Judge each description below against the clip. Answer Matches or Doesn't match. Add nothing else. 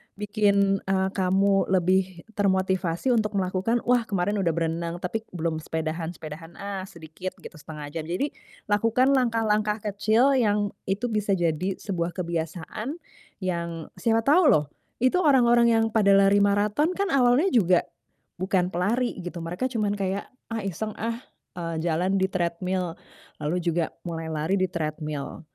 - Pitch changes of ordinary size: Matches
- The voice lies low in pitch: Doesn't match